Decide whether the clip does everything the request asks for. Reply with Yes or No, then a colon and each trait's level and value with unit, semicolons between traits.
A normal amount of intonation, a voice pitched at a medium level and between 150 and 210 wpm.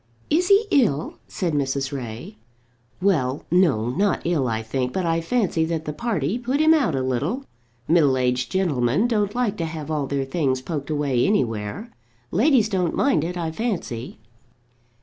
No: wide, 7.5 semitones; medium, 160 Hz; average, 170 wpm